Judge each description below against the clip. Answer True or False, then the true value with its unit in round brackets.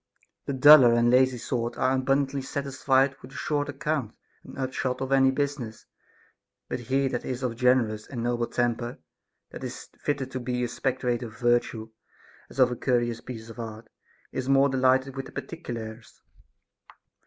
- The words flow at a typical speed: True (170 wpm)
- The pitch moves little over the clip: True (2.1 semitones)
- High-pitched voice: False (130 Hz)